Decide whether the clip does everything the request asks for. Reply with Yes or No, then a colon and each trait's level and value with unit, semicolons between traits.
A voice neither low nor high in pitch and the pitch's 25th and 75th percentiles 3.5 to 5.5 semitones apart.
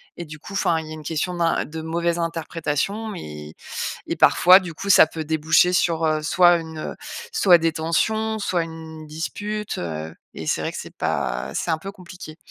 No: medium, 165 Hz; narrow, 2.4 semitones